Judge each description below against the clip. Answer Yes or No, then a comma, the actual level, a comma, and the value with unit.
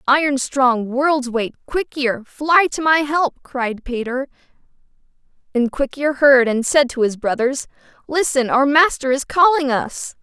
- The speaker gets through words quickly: No, average, 160 wpm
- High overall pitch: Yes, very high, 270 Hz